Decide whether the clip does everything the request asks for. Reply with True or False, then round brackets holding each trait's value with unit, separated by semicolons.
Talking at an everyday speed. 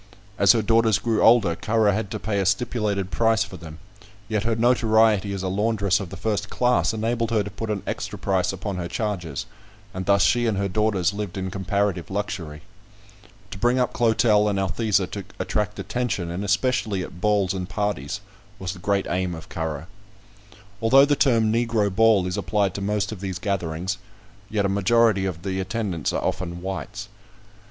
True (185 wpm)